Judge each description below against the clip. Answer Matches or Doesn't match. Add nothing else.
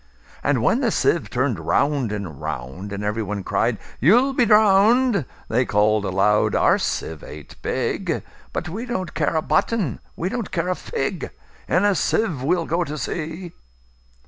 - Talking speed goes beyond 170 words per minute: Doesn't match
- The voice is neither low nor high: Matches